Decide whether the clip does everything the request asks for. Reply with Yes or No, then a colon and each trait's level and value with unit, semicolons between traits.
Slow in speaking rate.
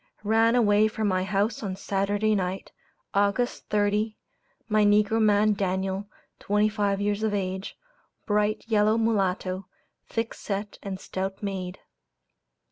Yes: slow, 125 wpm